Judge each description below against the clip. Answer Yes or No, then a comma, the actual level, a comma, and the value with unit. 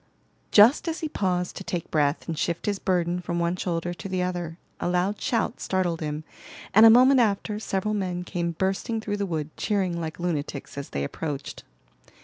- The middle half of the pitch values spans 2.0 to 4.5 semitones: Yes, average, 3.5 semitones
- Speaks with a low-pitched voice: No, medium, 180 Hz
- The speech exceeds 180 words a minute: Yes, average, 190 wpm